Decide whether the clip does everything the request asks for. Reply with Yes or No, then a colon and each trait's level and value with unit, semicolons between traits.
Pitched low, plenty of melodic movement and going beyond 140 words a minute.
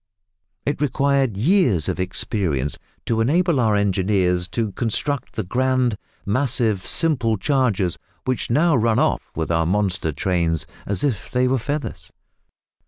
No: low, 110 Hz; wide, 6.2 semitones; slow, 135 wpm